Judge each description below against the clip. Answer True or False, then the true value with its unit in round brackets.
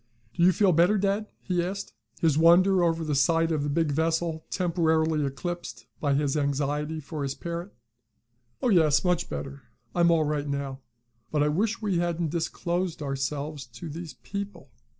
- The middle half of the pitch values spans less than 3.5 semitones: True (3.0 semitones)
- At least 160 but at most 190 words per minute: True (170 wpm)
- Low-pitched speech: False (160 Hz)